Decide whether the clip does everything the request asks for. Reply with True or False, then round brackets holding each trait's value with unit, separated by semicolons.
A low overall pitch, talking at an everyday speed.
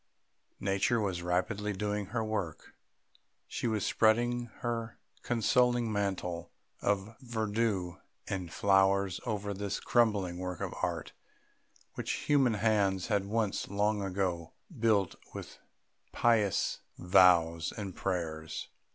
False (100 Hz; 110 wpm)